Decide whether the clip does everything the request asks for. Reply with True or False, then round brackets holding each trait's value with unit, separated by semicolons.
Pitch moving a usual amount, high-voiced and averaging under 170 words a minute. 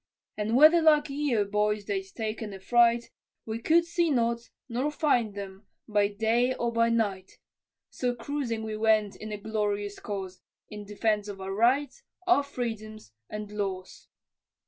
True (3.0 semitones; 220 Hz; 150 wpm)